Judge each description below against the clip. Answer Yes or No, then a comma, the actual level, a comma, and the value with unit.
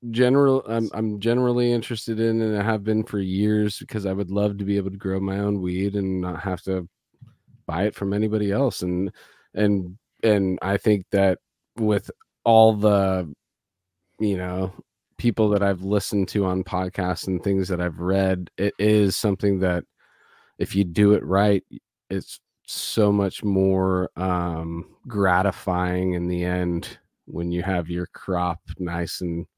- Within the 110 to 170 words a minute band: Yes, average, 165 wpm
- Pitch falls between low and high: No, low, 100 Hz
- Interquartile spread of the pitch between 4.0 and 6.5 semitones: No, narrow, 2.5 semitones